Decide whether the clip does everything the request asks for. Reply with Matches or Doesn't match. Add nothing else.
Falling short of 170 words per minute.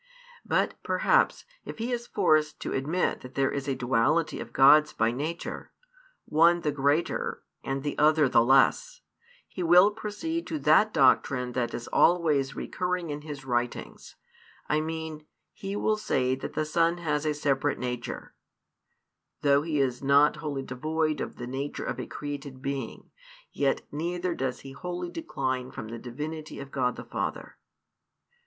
Matches